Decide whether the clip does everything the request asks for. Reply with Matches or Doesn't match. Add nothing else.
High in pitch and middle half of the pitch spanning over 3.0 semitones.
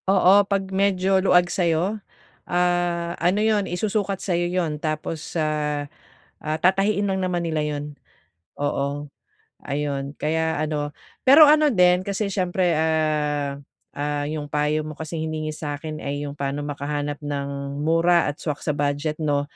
Doesn't match